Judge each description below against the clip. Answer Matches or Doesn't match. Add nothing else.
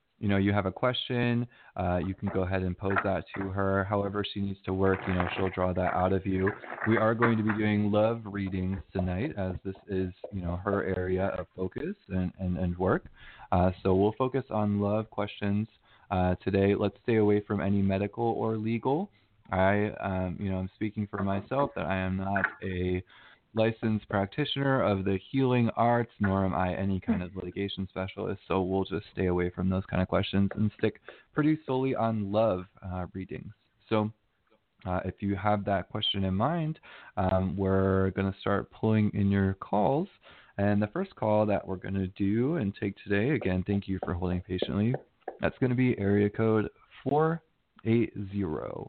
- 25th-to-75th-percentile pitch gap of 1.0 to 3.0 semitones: Matches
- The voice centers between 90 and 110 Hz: Matches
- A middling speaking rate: Matches